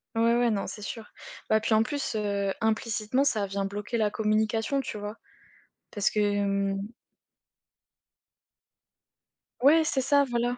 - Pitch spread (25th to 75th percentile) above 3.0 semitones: No, average, 2.7 semitones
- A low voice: No, high, 220 Hz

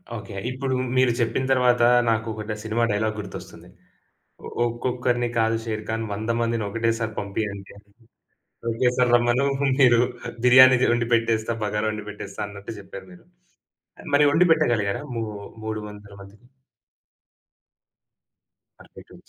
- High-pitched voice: No, low, 115 Hz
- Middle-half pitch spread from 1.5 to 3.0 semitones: Yes, narrow, 2.6 semitones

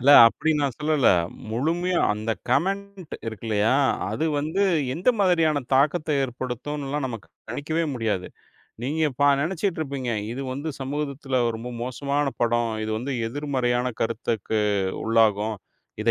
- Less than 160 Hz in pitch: Yes, low, 135 Hz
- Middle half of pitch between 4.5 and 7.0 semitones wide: Yes, average, 4.8 semitones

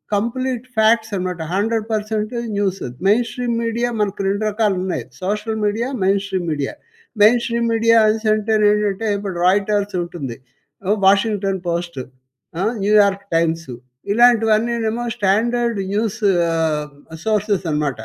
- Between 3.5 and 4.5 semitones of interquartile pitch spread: No, average, 2.7 semitones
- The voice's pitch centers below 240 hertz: Yes, high, 210 Hz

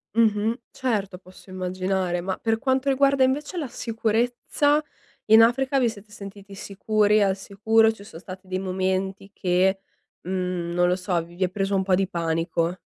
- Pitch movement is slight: No, average, 3.4 semitones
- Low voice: No, high, 195 Hz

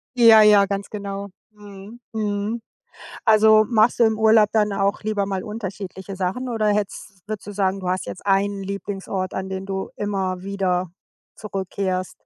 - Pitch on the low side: No, high, 200 Hz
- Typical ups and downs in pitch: No, narrow, 1.9 semitones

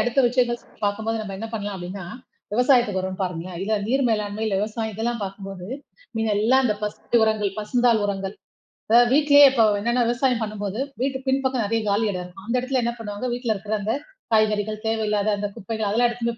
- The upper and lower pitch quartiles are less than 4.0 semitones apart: Yes, average, 2.9 semitones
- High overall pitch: Yes, high, 220 Hz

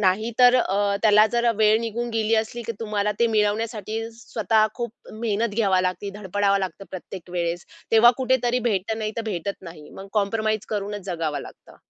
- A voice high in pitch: Yes, high, 210 Hz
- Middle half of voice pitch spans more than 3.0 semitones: No, narrow, 2.4 semitones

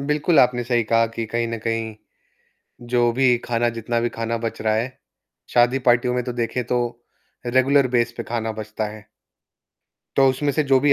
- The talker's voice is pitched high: No, low, 120 Hz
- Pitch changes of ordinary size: No, narrow, 1.9 semitones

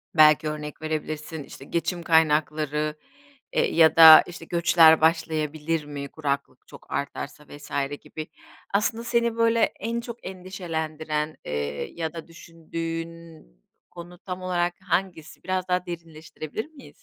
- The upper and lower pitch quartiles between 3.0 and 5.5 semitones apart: No, narrow, 2.6 semitones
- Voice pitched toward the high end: No, medium, 160 Hz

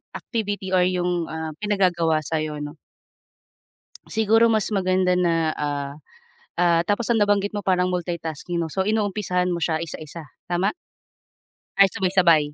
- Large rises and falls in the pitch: No, average, 3.6 semitones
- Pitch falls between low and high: Yes, medium, 180 Hz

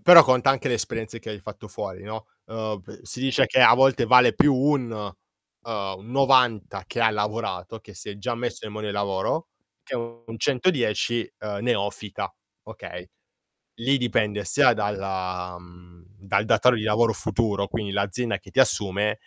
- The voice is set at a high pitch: No, low, 110 Hz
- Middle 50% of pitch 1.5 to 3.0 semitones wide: No, average, 3.4 semitones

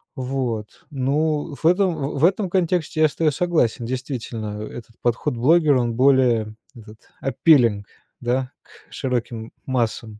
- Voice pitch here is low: Yes, low, 130 Hz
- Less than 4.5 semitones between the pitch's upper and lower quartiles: No, average, 4.9 semitones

